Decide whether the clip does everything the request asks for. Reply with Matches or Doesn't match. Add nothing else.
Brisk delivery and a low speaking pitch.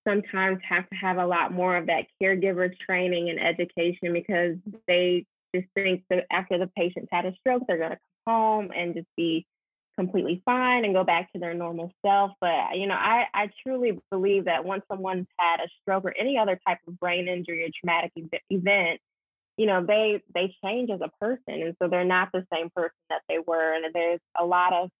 Doesn't match